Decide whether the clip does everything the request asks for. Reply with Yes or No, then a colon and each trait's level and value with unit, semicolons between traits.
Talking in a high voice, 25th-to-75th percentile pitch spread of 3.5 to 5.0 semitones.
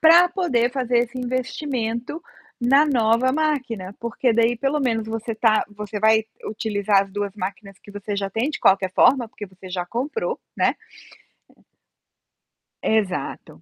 Yes: high, 225 Hz; average, 3.9 semitones